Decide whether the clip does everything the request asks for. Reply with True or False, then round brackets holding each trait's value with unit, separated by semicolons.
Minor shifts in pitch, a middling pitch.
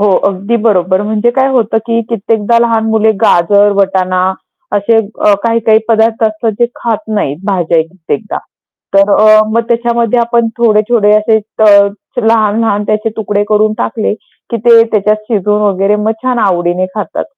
False (2.2 semitones; 215 Hz)